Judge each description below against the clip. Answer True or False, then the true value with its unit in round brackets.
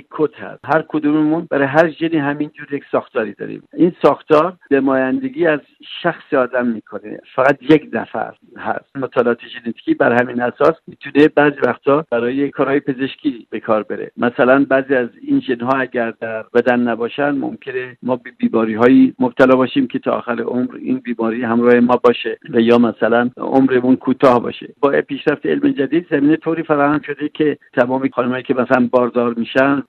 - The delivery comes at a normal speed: False (165 wpm)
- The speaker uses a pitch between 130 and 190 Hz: True (135 Hz)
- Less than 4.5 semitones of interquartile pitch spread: True (3.8 semitones)